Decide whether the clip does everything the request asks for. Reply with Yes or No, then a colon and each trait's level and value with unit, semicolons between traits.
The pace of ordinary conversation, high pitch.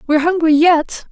Yes: average, 160 wpm; very high, 320 Hz